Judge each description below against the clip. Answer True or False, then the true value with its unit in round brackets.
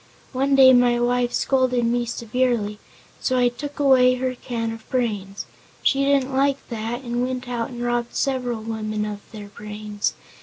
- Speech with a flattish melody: True (2.3 semitones)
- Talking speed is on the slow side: False (165 wpm)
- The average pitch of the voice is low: False (245 Hz)